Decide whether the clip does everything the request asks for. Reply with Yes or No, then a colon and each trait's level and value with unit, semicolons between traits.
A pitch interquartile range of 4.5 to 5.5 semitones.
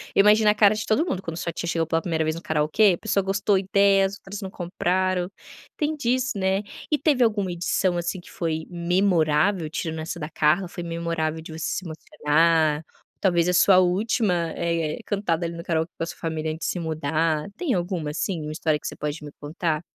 No: average, 3.4 semitones